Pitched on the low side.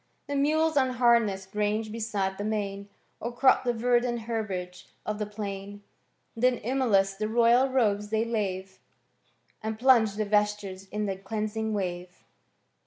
No: high, 215 Hz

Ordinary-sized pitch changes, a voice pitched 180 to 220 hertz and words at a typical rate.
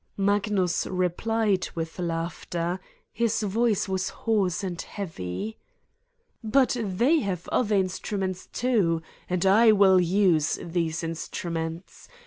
No: average, 3.6 semitones; high, 190 Hz; slow, 110 wpm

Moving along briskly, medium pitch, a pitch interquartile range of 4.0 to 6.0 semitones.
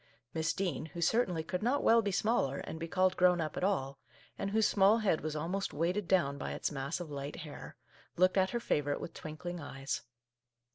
Yes: fast, 220 wpm; medium, 170 Hz; average, 4.4 semitones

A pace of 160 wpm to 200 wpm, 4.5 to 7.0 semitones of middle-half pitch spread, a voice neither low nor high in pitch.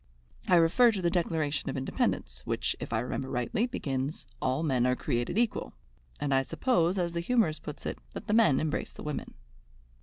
Yes: average, 190 wpm; average, 5.2 semitones; medium, 155 Hz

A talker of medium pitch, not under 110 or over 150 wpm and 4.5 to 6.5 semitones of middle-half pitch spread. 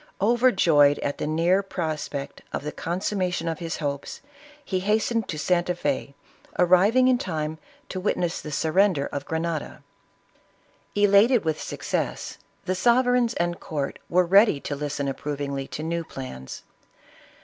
Yes: medium, 170 Hz; average, 140 wpm; average, 4.9 semitones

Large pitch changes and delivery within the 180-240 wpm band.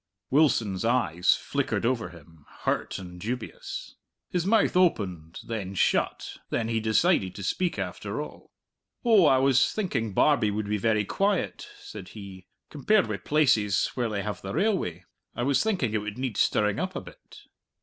No: wide, 7.0 semitones; average, 165 wpm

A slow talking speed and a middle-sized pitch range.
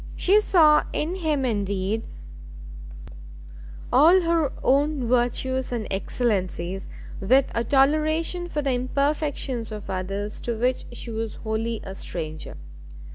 No: slow, 120 wpm; wide, 5.9 semitones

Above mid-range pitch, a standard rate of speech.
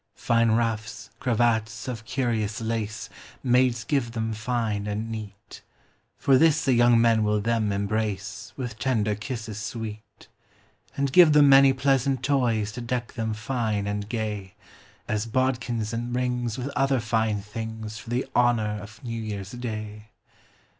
No: low, 115 Hz; average, 145 wpm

